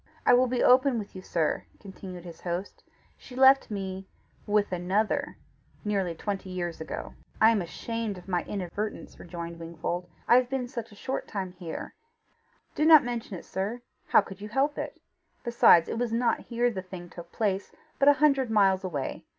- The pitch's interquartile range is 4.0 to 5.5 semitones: Yes, average, 5.0 semitones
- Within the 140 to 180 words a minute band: No, average, 190 wpm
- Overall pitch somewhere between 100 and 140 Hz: No, high, 200 Hz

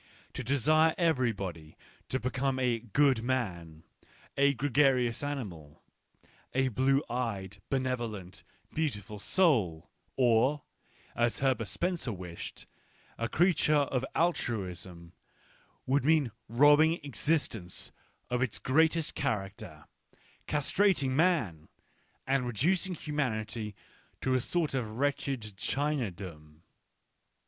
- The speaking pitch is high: No, low, 130 Hz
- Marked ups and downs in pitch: Yes, wide, 5.7 semitones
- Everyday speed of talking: No, slow, 110 wpm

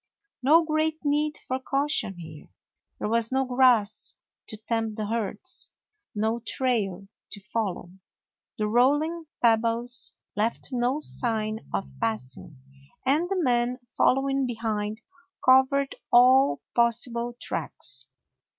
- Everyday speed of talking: No, slow, 115 wpm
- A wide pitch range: No, average, 3.7 semitones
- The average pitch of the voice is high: Yes, high, 240 Hz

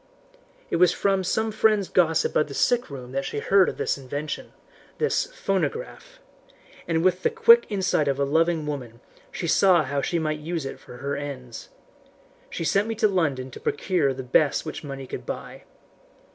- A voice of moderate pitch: Yes, medium, 160 Hz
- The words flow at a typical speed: Yes, average, 185 wpm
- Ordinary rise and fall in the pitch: No, wide, 5.8 semitones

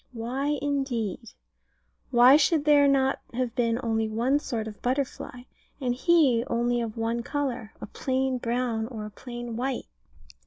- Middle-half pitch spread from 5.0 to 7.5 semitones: No, average, 2.8 semitones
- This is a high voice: Yes, high, 245 Hz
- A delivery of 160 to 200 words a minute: No, average, 150 wpm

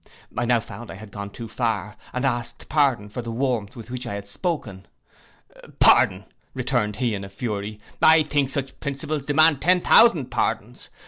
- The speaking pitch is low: Yes, low, 120 Hz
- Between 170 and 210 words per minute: Yes, average, 180 wpm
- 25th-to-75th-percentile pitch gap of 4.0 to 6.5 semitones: Yes, average, 5.0 semitones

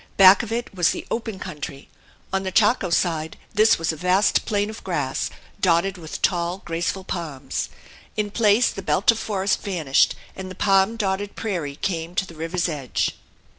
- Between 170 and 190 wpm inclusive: Yes, average, 175 wpm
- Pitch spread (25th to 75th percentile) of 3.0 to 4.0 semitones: Yes, average, 3.4 semitones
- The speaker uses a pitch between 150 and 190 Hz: Yes, medium, 185 Hz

